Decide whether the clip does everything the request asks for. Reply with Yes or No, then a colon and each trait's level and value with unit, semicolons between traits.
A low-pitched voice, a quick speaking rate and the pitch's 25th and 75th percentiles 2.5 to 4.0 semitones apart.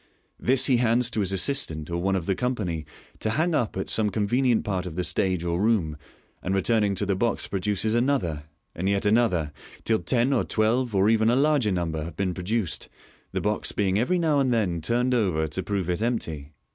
No: low, 105 Hz; fast, 210 wpm; average, 4.8 semitones